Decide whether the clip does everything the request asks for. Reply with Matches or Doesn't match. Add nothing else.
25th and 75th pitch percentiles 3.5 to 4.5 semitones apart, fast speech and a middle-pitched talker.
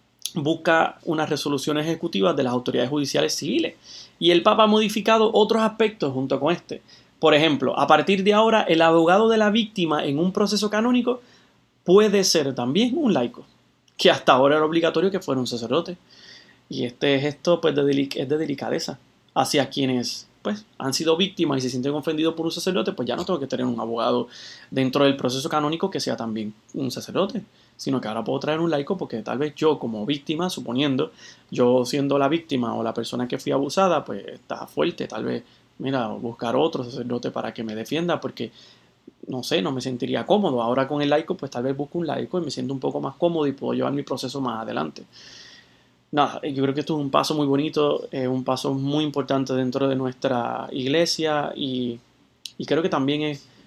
Matches